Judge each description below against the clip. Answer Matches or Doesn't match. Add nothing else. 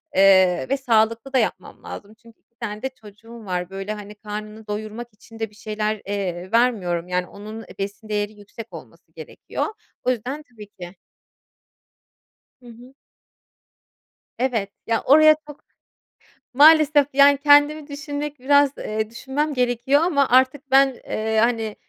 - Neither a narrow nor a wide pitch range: Matches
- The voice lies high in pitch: Matches